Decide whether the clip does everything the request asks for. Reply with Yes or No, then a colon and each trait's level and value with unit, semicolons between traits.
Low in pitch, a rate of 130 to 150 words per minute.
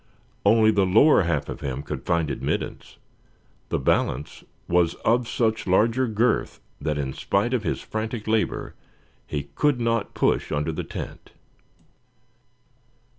Yes: low, 105 Hz; slow, 135 wpm